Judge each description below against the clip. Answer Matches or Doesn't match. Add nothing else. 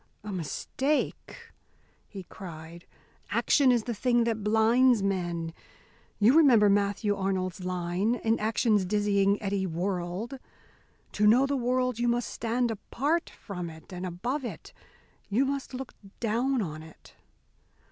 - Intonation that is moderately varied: Matches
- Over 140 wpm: Doesn't match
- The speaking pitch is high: Matches